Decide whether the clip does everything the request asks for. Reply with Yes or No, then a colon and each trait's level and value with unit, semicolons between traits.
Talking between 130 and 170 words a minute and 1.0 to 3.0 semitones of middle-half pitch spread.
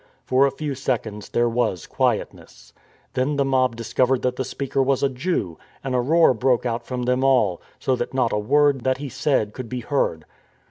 No: average, 195 wpm; narrow, 2.4 semitones